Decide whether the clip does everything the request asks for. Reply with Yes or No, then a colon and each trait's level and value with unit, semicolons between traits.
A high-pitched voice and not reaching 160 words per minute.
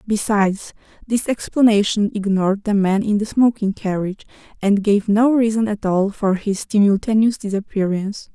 Yes: high, 205 Hz; average, 145 wpm